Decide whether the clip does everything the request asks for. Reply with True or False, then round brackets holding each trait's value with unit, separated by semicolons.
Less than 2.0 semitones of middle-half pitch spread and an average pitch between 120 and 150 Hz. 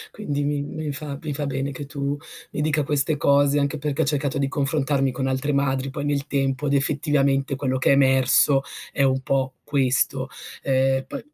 True (1.3 semitones; 140 Hz)